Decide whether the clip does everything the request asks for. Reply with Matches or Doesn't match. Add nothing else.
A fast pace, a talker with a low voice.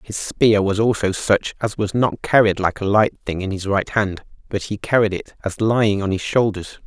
Matches